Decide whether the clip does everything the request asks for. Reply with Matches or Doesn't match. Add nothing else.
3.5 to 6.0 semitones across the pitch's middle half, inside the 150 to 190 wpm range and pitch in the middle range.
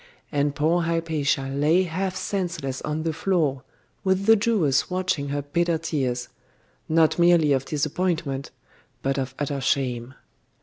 Doesn't match